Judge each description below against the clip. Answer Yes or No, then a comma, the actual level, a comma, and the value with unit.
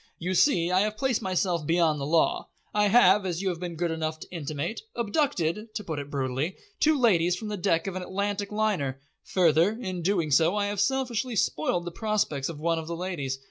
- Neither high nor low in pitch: Yes, medium, 180 Hz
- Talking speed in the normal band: No, fast, 215 wpm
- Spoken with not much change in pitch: No, average, 4.3 semitones